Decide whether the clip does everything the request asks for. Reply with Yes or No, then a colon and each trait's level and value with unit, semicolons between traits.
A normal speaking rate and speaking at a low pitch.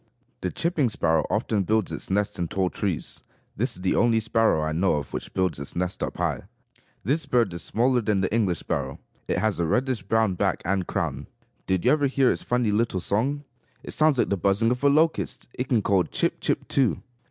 No: fast, 215 wpm; low, 105 Hz